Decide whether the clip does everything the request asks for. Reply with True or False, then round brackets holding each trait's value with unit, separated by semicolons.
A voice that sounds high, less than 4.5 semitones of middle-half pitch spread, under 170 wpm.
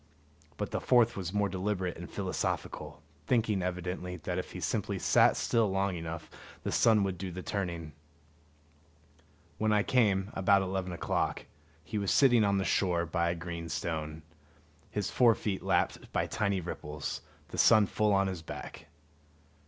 False (95 Hz; 3.0 semitones; 160 wpm)